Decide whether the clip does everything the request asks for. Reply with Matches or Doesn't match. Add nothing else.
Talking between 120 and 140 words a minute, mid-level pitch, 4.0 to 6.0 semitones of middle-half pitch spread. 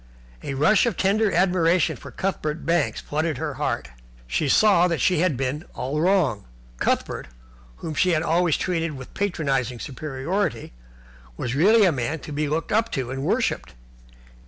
Doesn't match